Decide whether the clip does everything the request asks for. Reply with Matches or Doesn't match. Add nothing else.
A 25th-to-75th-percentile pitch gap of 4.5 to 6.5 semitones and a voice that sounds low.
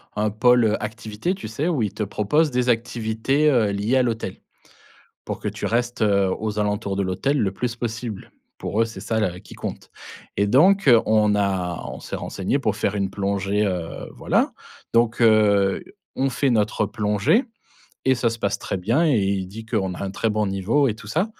Doesn't match